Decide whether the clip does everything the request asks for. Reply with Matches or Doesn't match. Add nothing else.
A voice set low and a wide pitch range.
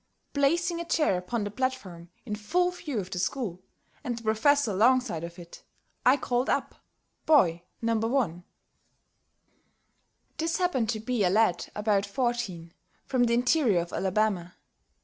Doesn't match